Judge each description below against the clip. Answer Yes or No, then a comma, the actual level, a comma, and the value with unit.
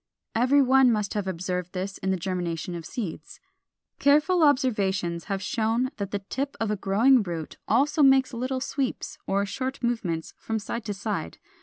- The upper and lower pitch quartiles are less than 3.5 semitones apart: No, wide, 5.5 semitones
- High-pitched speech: Yes, high, 210 Hz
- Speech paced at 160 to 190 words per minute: Yes, average, 170 wpm